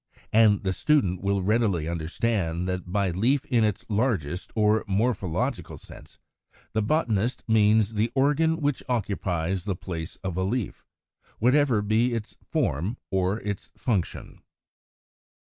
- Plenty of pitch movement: No, average, 4.0 semitones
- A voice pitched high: No, low, 105 Hz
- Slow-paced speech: Yes, slow, 130 wpm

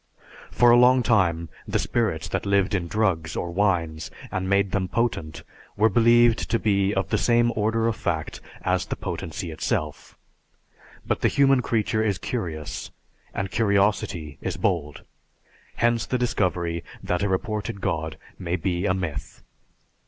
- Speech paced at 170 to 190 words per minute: No, average, 150 wpm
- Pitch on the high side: No, low, 100 Hz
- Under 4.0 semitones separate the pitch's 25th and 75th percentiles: No, average, 4.8 semitones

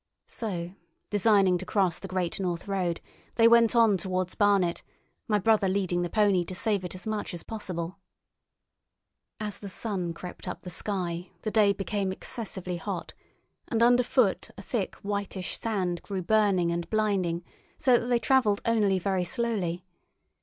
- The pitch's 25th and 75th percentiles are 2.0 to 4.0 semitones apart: Yes, average, 3.2 semitones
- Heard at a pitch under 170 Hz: No, high, 195 Hz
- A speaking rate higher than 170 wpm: No, average, 160 wpm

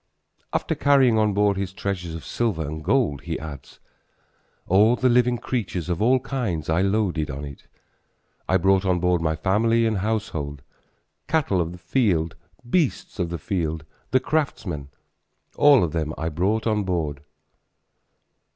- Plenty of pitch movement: Yes, wide, 5.9 semitones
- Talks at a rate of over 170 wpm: No, average, 155 wpm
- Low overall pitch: Yes, very low, 95 Hz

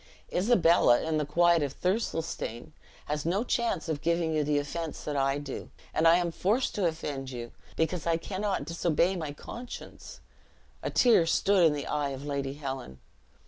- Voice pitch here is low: No, medium, 160 Hz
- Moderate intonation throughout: Yes, average, 3.5 semitones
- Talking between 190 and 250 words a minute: No, average, 175 wpm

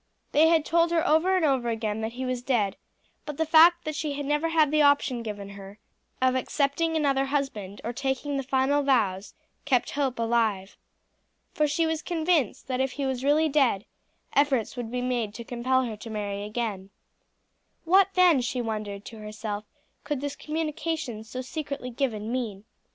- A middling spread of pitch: Yes, average, 5.0 semitones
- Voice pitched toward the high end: Yes, very high, 260 Hz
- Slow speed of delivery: No, average, 180 wpm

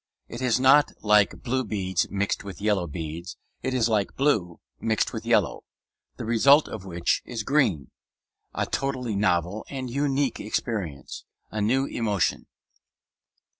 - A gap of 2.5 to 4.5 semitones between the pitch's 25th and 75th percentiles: No, wide, 5.4 semitones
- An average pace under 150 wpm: Yes, average, 140 wpm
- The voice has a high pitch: No, low, 110 Hz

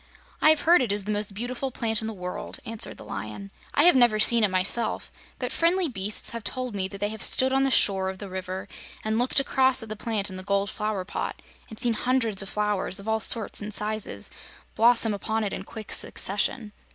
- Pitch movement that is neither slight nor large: Yes, average, 3.4 semitones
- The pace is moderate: No, fast, 225 wpm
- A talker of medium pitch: No, high, 215 Hz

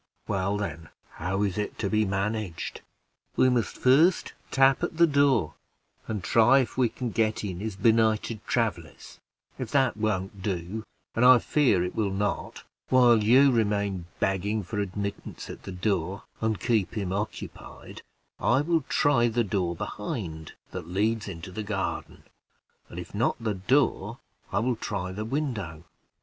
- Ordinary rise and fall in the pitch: Yes, average, 3.7 semitones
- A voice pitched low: Yes, low, 105 Hz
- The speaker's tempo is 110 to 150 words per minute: No, average, 160 wpm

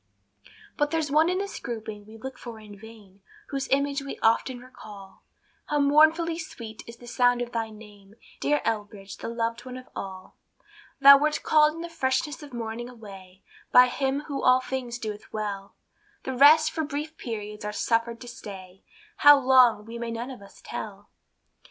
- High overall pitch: Yes, high, 240 Hz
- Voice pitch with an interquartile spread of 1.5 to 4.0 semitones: No, average, 4.7 semitones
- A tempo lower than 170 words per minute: No, average, 180 wpm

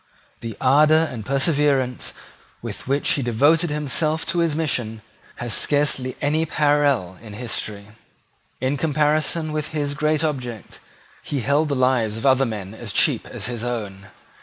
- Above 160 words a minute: No, average, 150 wpm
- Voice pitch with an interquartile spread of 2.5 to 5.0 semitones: Yes, average, 4.2 semitones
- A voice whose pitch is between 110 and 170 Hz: Yes, medium, 140 Hz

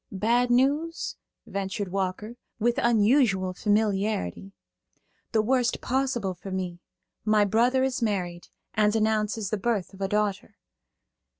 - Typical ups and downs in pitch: Yes, average, 3.6 semitones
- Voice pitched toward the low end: No, high, 210 Hz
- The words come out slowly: Yes, slow, 120 wpm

